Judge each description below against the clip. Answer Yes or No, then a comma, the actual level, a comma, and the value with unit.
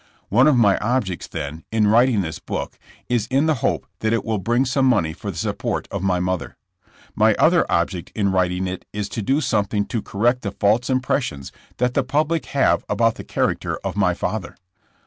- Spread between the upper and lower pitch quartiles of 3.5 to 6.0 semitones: Yes, average, 4.8 semitones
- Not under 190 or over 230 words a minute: Yes, average, 200 wpm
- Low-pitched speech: Yes, low, 110 Hz